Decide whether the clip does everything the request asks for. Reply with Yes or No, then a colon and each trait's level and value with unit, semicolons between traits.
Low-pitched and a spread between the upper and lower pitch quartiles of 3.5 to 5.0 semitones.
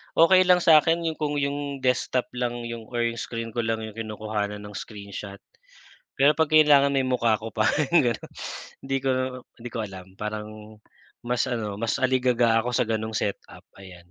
Yes: low, 120 Hz; average, 4.2 semitones